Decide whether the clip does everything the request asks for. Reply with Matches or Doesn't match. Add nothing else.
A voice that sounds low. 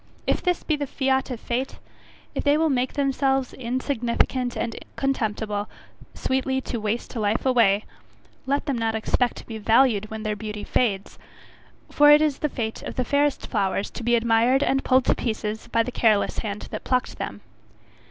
Doesn't match